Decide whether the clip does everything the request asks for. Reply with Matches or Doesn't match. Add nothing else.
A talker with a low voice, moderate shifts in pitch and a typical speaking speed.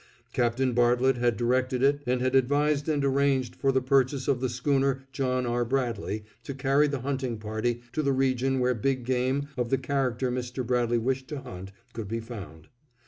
Doesn't match